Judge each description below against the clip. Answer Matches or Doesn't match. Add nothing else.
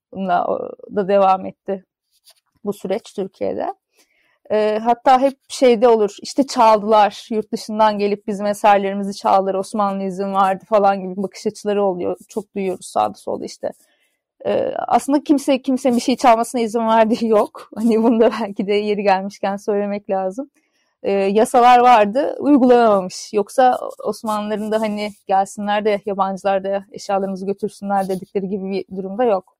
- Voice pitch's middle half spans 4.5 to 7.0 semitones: Doesn't match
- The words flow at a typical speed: Doesn't match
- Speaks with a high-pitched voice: Matches